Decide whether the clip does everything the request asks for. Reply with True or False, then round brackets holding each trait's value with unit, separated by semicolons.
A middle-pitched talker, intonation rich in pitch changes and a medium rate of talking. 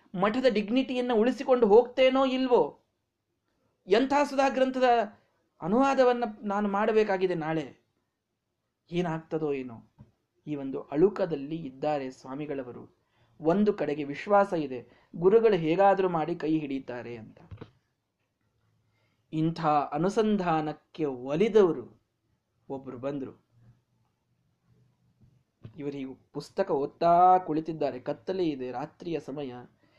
True (150 Hz; 7.8 semitones; 85 wpm)